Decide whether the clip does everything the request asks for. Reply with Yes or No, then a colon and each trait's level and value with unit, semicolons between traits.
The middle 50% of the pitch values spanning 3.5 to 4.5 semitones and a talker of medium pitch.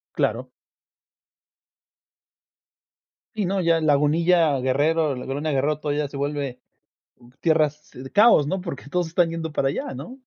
No: average, 3.0 semitones; medium, 155 Hz